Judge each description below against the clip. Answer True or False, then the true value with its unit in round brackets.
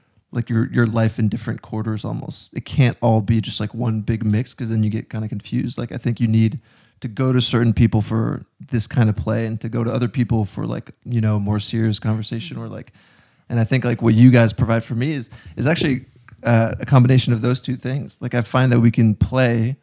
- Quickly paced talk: True (245 wpm)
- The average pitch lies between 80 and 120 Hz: True (115 Hz)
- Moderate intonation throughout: False (2.0 semitones)